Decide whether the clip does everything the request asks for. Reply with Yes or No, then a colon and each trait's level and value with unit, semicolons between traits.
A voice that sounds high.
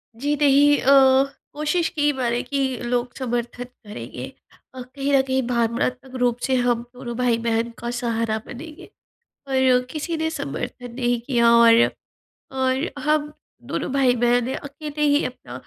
Yes: very high, 250 Hz